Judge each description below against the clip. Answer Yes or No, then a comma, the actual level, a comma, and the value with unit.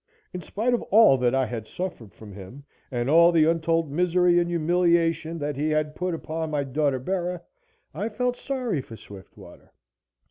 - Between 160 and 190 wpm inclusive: Yes, average, 175 wpm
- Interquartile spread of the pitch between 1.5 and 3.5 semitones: No, average, 4.5 semitones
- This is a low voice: No, medium, 165 Hz